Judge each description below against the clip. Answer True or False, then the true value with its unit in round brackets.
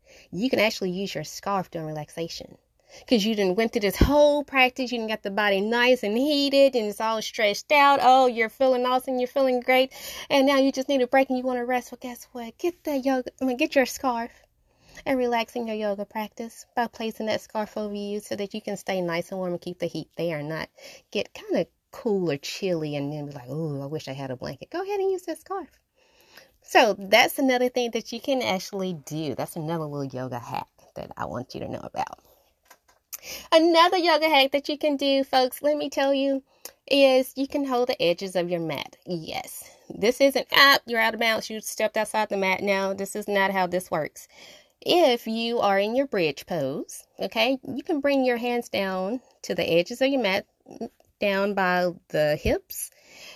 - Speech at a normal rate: False (220 wpm)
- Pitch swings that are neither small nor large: False (5.8 semitones)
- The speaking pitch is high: True (230 Hz)